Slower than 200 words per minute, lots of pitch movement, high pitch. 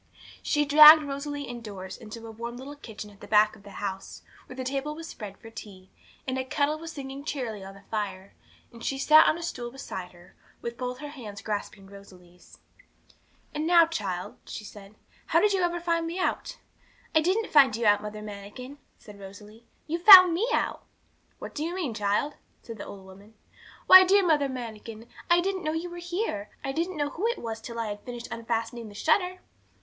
No: fast, 205 wpm; wide, 6.9 semitones; high, 245 Hz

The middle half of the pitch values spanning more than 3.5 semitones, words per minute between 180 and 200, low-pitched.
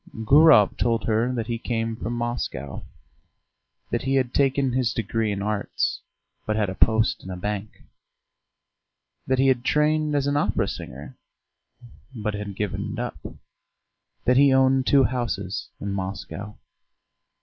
No: average, 4.1 semitones; average, 150 wpm; low, 115 Hz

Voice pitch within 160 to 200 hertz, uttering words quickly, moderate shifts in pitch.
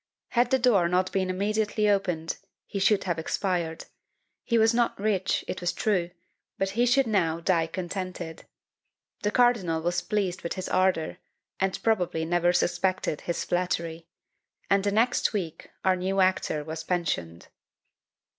No: medium, 185 Hz; average, 150 wpm; average, 3.4 semitones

